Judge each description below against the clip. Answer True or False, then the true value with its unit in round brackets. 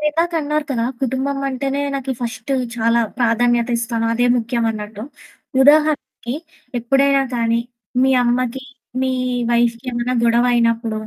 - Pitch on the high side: True (240 Hz)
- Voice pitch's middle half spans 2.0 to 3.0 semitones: True (2.7 semitones)